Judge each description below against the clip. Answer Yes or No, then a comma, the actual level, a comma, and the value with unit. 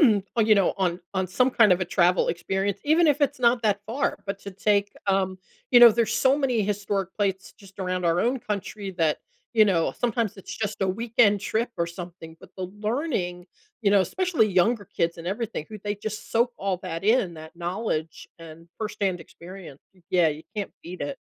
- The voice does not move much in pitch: No, average, 3.9 semitones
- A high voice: Yes, high, 200 Hz